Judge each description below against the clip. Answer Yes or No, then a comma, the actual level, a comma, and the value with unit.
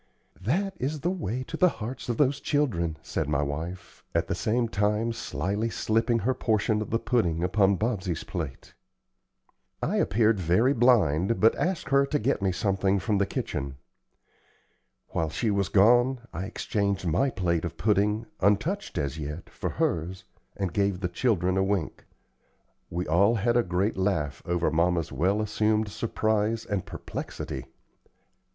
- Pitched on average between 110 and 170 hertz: No, low, 100 Hz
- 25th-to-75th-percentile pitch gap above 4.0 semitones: Yes, average, 4.7 semitones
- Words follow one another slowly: No, average, 160 wpm